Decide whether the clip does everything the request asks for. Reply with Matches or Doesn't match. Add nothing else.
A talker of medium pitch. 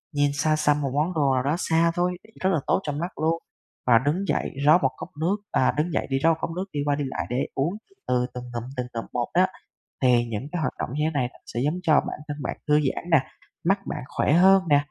Matches